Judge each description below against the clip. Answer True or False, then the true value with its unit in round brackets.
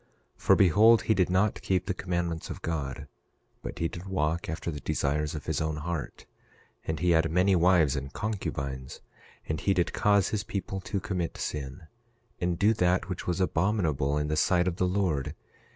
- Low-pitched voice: True (85 Hz)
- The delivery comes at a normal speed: True (190 wpm)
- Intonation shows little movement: False (3.6 semitones)